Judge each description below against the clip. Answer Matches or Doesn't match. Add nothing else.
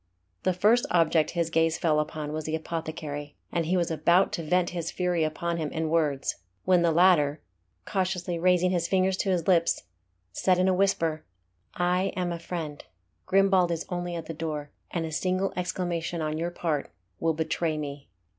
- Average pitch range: Doesn't match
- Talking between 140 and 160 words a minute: Doesn't match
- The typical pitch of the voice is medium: Matches